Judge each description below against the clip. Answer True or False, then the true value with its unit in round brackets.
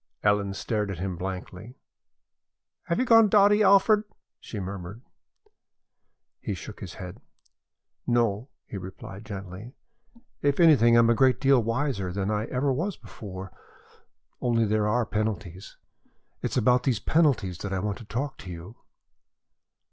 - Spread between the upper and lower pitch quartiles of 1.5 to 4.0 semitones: False (5.3 semitones)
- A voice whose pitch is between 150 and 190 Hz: False (110 Hz)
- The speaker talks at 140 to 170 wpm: True (150 wpm)